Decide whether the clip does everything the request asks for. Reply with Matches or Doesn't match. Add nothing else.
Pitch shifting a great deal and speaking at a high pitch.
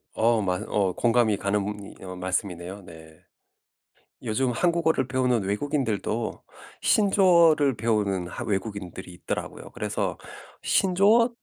Doesn't match